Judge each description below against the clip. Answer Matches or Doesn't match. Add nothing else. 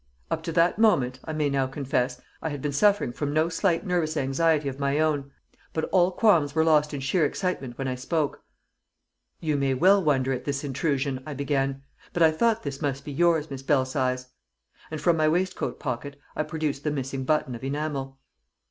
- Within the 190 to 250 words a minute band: Matches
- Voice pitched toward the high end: Doesn't match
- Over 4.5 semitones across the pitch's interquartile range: Doesn't match